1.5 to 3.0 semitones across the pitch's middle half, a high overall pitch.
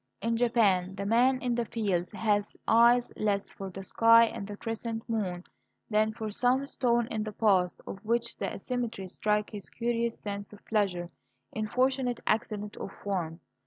Yes: average, 2.7 semitones; high, 215 Hz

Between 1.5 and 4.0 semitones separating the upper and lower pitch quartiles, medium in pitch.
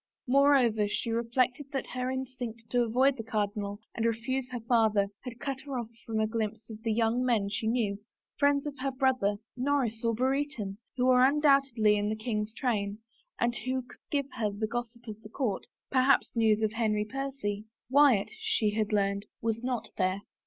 No: average, 3.3 semitones; high, 230 Hz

